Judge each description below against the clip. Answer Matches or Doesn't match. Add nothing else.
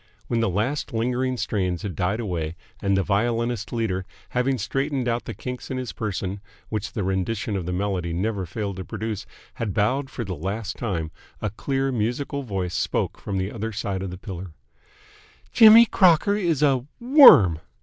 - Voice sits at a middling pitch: Doesn't match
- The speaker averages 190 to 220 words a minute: Doesn't match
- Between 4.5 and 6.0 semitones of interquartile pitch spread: Matches